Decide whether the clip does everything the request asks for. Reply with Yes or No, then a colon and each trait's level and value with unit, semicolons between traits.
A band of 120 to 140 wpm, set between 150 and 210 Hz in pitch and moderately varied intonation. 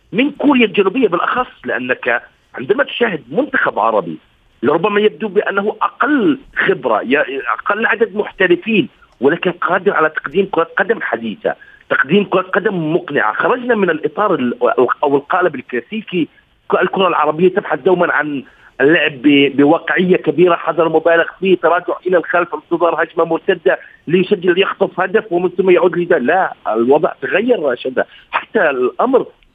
Yes: average, 130 wpm; medium, 185 Hz; average, 4.2 semitones